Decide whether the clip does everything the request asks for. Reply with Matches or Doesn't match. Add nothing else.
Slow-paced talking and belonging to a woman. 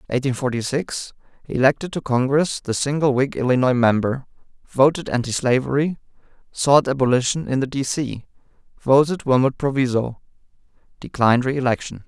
Doesn't match